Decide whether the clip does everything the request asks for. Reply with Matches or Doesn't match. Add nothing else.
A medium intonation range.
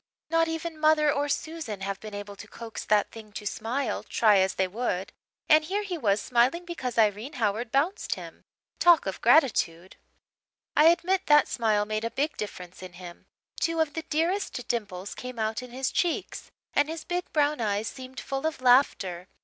Doesn't match